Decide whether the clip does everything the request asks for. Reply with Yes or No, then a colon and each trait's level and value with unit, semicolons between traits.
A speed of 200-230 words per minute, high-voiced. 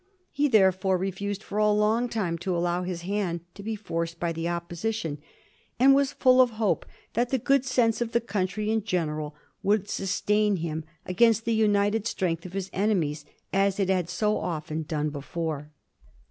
No: average, 180 wpm; high, 195 Hz